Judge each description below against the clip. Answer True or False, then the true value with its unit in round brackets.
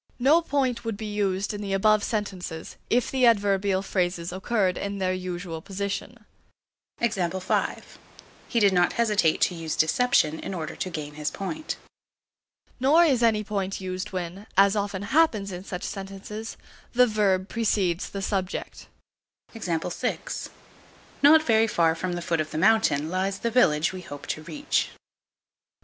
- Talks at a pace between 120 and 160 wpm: True (150 wpm)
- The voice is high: True (195 Hz)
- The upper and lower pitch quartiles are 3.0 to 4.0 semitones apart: True (3.6 semitones)